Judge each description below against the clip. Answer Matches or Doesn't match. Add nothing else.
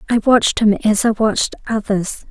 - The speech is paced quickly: Doesn't match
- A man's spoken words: Doesn't match